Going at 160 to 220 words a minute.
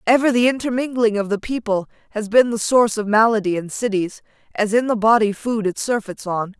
Yes: average, 200 wpm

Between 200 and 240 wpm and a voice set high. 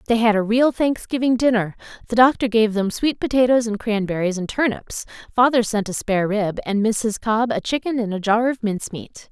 Yes: fast, 205 wpm; high, 225 Hz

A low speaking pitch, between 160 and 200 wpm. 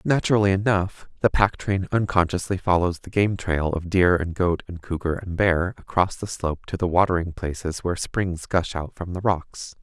Yes: very low, 90 Hz; average, 195 wpm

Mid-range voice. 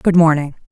Yes: medium, 160 Hz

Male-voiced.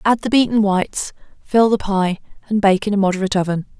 No: female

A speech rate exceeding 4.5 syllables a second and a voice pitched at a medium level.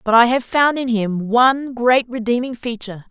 No: 5.0 syllables/s; high, 240 Hz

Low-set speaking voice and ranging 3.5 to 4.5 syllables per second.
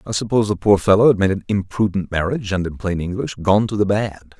No: low, 100 Hz; 6.2 syllables/s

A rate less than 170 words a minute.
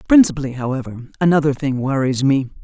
Yes: slow, 135 wpm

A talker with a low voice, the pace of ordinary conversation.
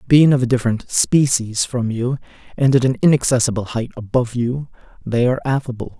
Yes: low, 125 Hz; average, 170 wpm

